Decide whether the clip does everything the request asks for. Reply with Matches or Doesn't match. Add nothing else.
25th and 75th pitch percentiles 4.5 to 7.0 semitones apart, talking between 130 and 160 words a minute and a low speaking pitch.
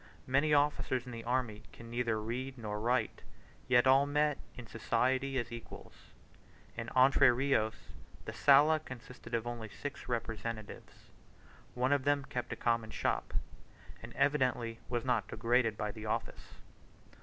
Doesn't match